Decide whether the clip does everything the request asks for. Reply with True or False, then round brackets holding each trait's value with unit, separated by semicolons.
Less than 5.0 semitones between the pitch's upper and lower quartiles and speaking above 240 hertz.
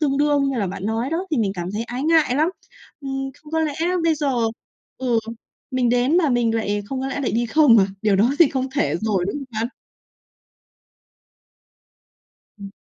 True (4.6 semitones; 260 Hz)